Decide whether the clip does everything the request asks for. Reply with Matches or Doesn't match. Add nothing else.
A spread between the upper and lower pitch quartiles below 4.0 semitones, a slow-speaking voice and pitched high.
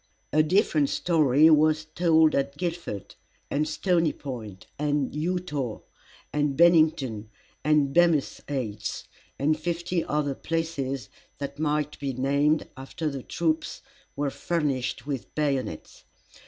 Doesn't match